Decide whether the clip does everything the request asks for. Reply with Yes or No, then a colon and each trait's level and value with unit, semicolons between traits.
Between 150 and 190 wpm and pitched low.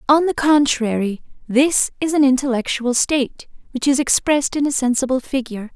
No: average, 155 wpm; very high, 265 Hz